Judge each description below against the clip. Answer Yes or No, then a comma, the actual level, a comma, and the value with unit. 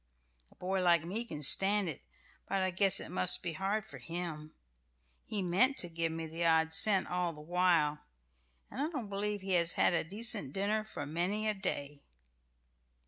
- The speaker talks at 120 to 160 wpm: No, average, 190 wpm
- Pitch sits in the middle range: Yes, medium, 180 Hz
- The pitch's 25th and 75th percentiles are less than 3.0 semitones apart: No, average, 3.7 semitones